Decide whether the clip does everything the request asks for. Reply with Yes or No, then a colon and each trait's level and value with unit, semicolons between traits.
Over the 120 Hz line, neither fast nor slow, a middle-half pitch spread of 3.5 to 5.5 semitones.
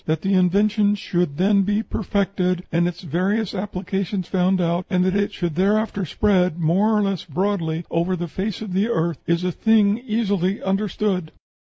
No: high, 190 Hz; average, 175 wpm; average, 2.7 semitones